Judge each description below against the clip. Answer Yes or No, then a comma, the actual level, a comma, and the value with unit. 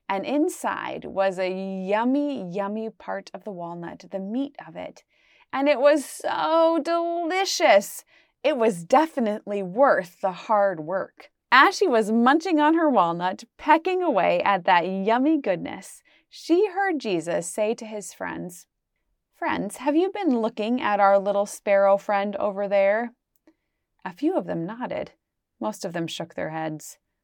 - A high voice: Yes, high, 220 Hz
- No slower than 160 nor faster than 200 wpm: No, average, 150 wpm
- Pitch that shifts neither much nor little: No, wide, 7.5 semitones